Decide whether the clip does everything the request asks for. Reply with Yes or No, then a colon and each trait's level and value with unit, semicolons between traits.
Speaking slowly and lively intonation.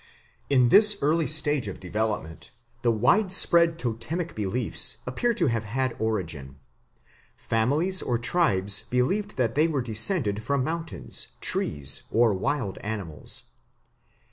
Yes: slow, 120 wpm; wide, 7.2 semitones